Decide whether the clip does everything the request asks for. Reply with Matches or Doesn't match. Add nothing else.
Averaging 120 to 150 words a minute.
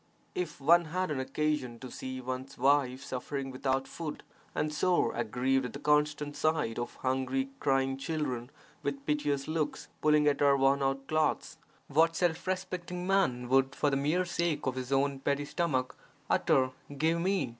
Doesn't match